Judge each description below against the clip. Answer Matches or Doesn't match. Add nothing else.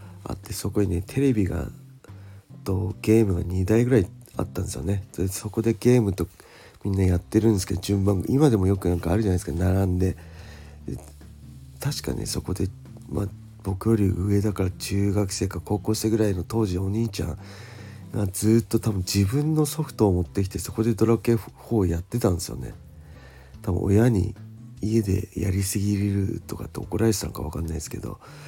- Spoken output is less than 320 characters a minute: Doesn't match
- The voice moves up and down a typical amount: Matches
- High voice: Doesn't match